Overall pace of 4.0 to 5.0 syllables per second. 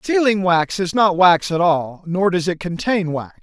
Yes: 4.3 syllables/s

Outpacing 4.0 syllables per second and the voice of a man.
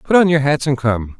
Yes: 5.5 syllables/s; male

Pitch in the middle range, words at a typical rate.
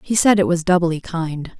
No: medium, 170 Hz; fast, 225 wpm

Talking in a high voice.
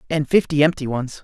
No: medium, 150 Hz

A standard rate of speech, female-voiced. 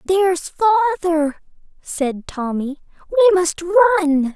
No: slow, 95 wpm; female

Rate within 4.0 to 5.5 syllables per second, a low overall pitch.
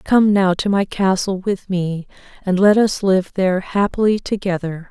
No: 4.5 syllables/s; high, 190 Hz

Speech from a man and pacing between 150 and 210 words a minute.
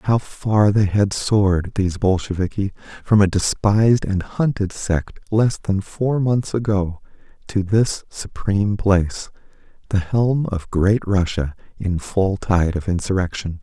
No: male; average, 140 wpm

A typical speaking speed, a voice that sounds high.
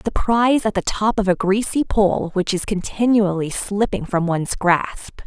Yes: average, 180 wpm; high, 200 Hz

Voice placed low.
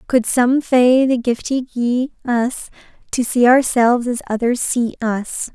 No: high, 245 Hz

